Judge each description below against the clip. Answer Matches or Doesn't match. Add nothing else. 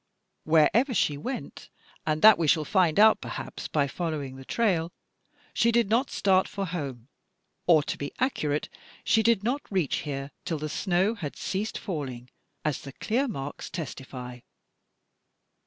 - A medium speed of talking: Matches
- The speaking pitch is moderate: Matches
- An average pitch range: Doesn't match